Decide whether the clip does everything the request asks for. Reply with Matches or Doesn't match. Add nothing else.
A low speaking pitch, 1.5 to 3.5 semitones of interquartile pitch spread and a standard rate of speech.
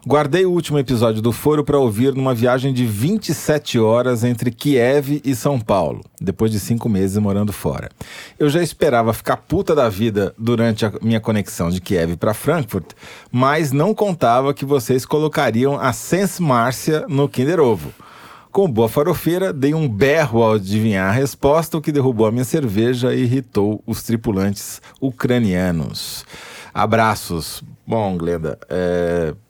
Doesn't match